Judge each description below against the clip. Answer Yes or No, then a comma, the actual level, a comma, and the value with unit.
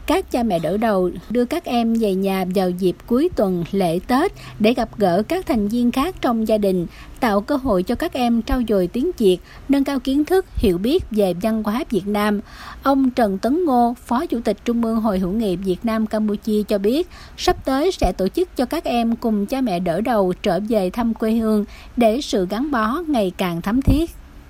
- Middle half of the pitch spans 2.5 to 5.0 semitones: Yes, average, 4.7 semitones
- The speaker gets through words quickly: No, average, 220 wpm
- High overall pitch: Yes, high, 225 Hz